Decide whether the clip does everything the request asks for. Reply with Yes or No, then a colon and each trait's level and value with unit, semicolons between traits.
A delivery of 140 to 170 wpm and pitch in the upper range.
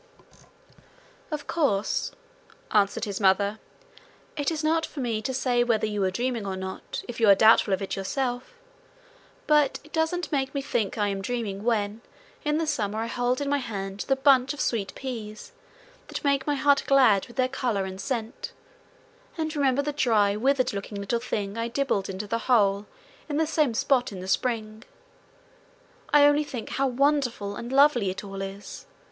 No: average, 180 wpm; high, 240 Hz